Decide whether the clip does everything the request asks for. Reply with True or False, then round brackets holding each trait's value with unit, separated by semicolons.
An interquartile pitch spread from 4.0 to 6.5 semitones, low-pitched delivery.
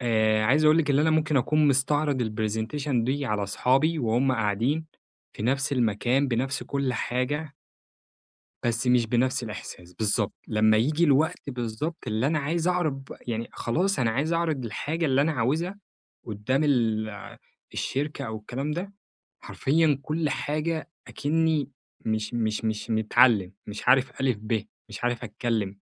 True (5.2 semitones; 130 Hz)